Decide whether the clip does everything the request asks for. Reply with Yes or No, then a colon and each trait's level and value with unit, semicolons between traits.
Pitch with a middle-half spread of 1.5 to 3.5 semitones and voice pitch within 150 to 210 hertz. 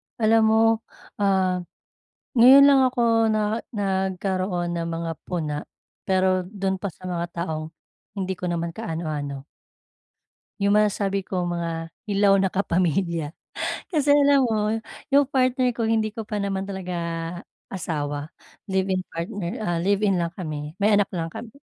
No: average, 4.0 semitones; high, 190 Hz